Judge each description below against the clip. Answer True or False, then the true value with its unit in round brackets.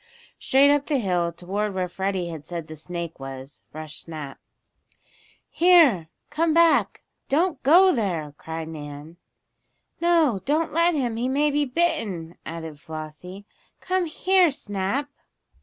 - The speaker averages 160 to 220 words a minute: False (135 wpm)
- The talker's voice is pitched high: True (195 Hz)